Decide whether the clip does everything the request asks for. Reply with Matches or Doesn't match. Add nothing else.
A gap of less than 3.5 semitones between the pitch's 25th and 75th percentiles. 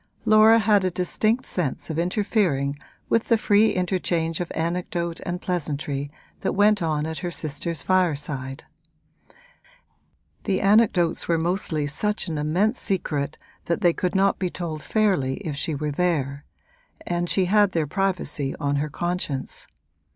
Doesn't match